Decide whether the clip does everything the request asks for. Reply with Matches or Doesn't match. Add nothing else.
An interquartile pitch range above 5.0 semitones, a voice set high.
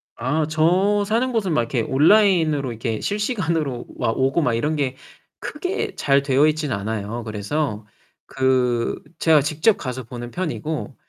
Doesn't match